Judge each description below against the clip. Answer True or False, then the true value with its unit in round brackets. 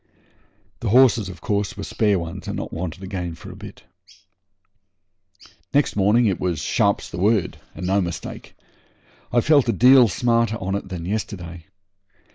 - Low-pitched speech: True (100 Hz)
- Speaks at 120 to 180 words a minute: True (160 wpm)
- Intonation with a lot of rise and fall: False (4.2 semitones)